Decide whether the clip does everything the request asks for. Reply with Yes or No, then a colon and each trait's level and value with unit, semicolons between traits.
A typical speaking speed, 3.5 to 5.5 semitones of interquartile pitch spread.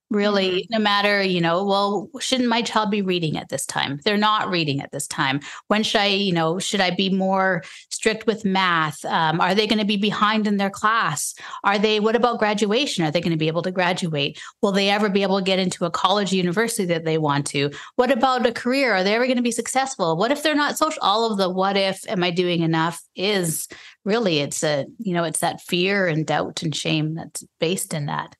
No: fast, 240 wpm; average, 4.2 semitones